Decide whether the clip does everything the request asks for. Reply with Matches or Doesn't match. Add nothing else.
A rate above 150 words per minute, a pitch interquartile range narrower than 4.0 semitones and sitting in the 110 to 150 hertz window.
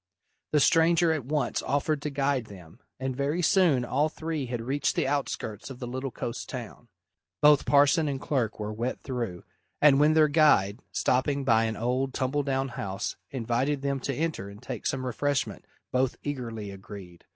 Matches